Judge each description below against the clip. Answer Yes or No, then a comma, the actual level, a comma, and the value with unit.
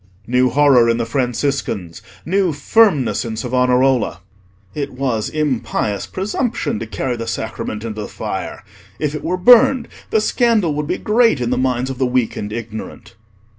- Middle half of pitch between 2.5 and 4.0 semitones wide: No, average, 4.9 semitones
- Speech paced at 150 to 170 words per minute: Yes, average, 165 wpm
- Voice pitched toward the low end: Yes, low, 130 Hz